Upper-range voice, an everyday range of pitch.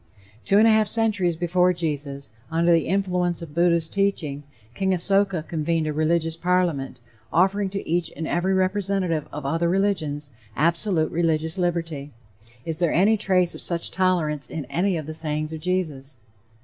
No: medium, 170 Hz; average, 3.1 semitones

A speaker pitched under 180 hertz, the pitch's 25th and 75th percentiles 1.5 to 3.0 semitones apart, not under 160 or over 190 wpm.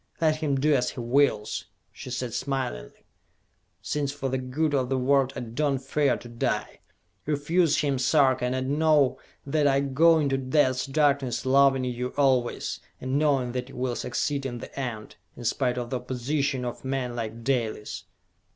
Yes: low, 135 Hz; narrow, 2.4 semitones; average, 175 wpm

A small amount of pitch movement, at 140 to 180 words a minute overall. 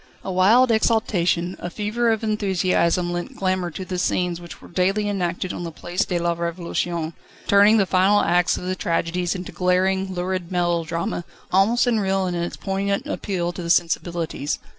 Yes: narrow, 2.1 semitones; average, 170 wpm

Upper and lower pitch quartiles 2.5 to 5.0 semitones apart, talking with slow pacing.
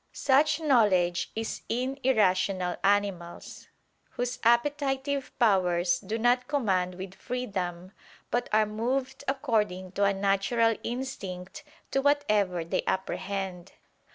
No: wide, 5.5 semitones; slow, 110 wpm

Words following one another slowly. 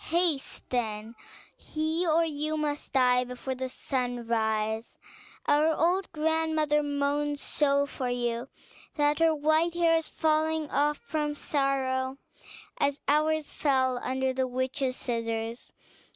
Yes: slow, 120 wpm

